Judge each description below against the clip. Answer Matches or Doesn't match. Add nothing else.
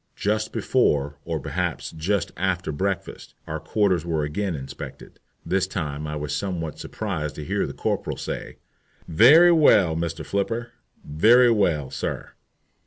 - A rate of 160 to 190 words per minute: Doesn't match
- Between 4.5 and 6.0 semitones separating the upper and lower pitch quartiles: Matches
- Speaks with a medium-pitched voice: Doesn't match